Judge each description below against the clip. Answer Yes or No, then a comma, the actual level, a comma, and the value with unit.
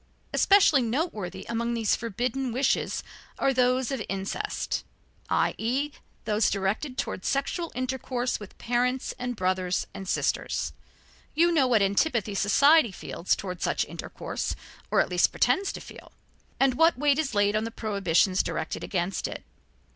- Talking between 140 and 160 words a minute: Yes, average, 145 wpm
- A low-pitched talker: No, high, 240 Hz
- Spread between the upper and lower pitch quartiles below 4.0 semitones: No, average, 5.2 semitones